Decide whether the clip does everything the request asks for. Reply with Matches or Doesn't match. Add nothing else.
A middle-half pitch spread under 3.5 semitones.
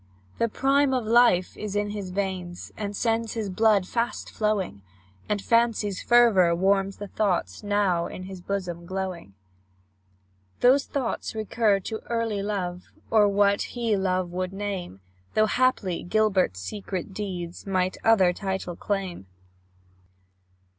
Matches